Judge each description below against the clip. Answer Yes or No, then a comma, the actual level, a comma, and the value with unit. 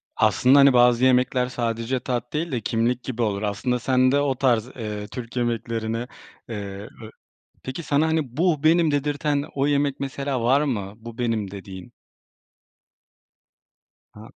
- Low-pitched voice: Yes, low, 125 Hz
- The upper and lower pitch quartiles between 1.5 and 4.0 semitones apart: Yes, average, 3.5 semitones